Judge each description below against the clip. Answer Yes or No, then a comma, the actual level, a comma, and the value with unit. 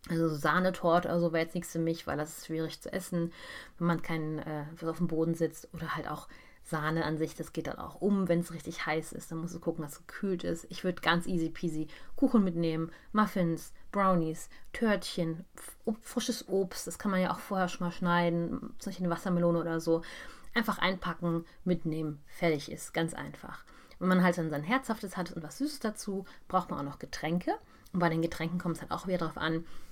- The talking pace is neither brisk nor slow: No, fast, 220 wpm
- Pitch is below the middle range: No, medium, 170 Hz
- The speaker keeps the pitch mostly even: Yes, narrow, 2.2 semitones